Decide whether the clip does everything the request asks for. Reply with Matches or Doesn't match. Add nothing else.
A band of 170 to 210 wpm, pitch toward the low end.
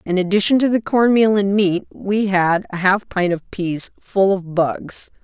Doesn't match